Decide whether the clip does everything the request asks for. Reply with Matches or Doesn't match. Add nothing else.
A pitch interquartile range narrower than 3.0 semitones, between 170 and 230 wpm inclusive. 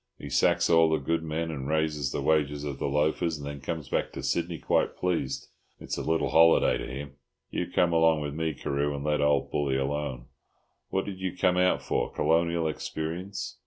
Matches